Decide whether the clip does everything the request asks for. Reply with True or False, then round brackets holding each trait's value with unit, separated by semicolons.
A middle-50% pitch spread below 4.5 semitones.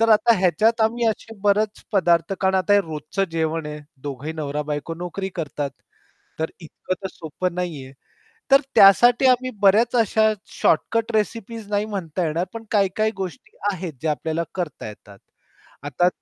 False (5.4 semitones)